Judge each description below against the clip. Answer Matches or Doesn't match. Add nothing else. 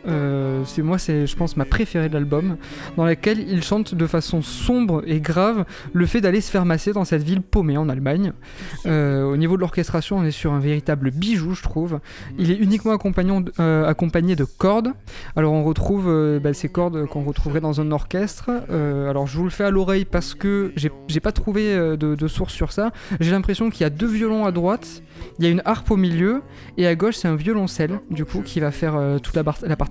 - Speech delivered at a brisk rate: Matches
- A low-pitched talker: Doesn't match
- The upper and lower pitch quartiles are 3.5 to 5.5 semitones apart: Matches